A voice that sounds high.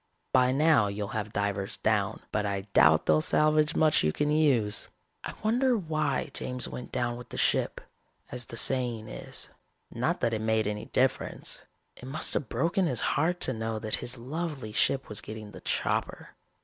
No: low, 120 Hz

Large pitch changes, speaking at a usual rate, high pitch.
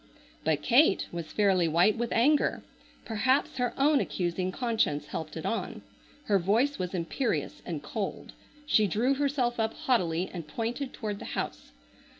Yes: wide, 6.1 semitones; average, 150 wpm; high, 215 Hz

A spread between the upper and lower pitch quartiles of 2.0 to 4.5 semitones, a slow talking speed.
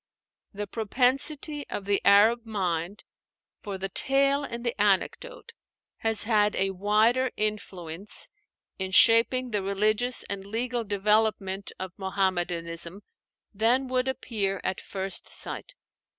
Yes: average, 3.7 semitones; slow, 120 wpm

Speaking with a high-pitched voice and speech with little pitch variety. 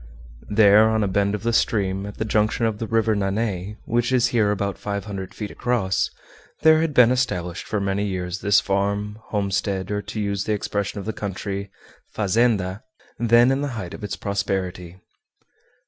No: low, 105 Hz; narrow, 2.3 semitones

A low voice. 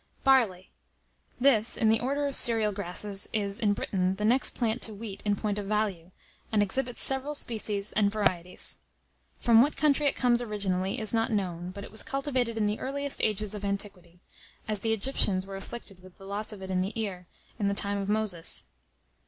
No: high, 210 Hz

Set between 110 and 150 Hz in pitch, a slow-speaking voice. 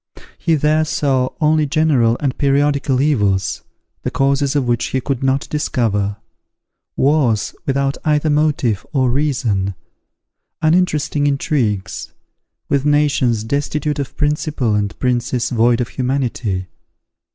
Yes: low, 135 Hz; slow, 120 wpm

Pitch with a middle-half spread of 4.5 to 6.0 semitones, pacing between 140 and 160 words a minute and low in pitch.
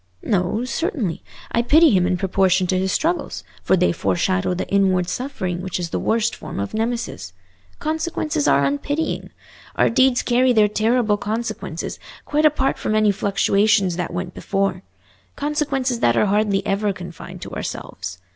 No: average, 5.3 semitones; average, 155 wpm; high, 205 Hz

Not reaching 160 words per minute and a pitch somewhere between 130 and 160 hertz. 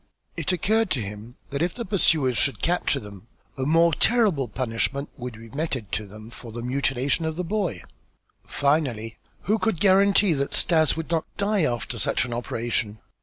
No: average, 175 wpm; medium, 140 Hz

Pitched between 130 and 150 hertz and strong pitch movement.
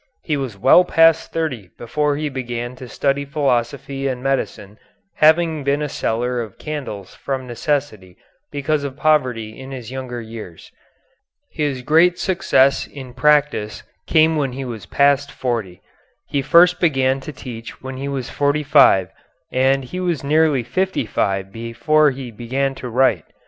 No: low, 135 Hz; average, 3.7 semitones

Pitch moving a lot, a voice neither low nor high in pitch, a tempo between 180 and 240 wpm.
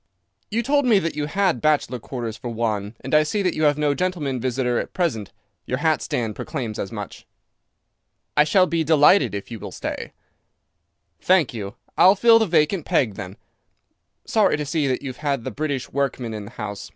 Yes: wide, 6.0 semitones; medium, 145 Hz; average, 195 wpm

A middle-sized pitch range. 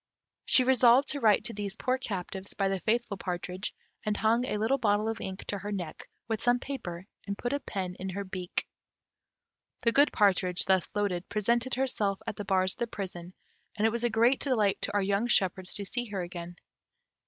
Yes: average, 3.9 semitones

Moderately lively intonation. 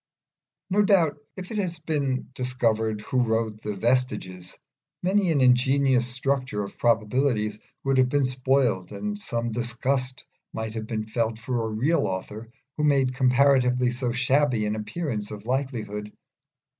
Yes: average, 3.8 semitones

